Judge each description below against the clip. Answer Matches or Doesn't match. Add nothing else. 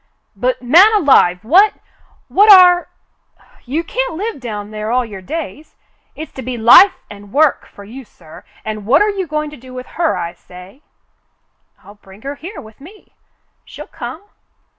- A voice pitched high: Matches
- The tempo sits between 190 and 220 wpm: Doesn't match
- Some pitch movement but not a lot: Doesn't match